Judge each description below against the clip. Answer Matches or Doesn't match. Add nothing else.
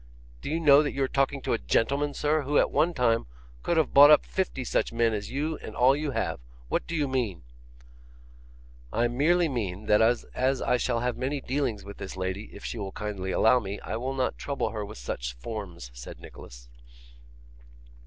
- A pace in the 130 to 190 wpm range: Doesn't match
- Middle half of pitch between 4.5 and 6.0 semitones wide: Matches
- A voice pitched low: Matches